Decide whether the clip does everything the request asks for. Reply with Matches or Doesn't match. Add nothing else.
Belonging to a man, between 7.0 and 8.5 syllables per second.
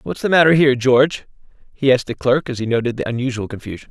Matches